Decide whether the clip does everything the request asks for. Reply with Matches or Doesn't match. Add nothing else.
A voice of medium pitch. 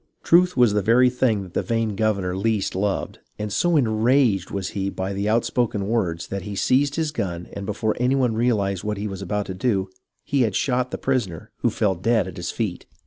Doesn't match